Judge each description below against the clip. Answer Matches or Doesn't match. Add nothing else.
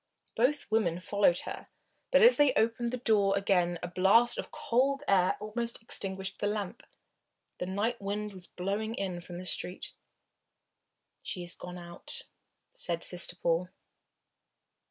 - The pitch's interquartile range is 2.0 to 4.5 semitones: Matches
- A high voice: Matches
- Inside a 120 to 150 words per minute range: Matches